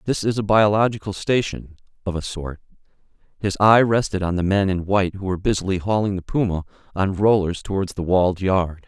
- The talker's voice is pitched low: Yes, very low, 95 Hz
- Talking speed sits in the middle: Yes, average, 180 wpm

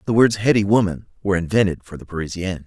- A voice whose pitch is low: Yes, very low, 95 Hz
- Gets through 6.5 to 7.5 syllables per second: Yes, 7.2 syllables/s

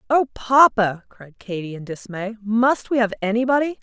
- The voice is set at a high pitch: Yes, high, 225 Hz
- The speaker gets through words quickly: No, average, 155 wpm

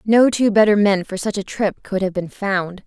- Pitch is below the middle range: No, high, 200 Hz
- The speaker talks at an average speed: No, fast, 250 wpm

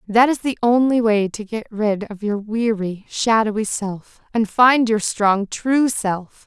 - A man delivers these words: No, female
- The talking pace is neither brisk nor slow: Yes, average, 175 wpm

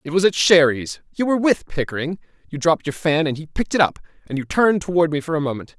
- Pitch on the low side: No, medium, 160 Hz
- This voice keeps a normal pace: No, fast, 250 wpm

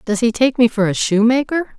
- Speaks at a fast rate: Yes, fast, 235 wpm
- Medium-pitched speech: No, high, 235 Hz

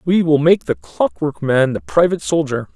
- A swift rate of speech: No, average, 195 wpm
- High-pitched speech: No, low, 135 Hz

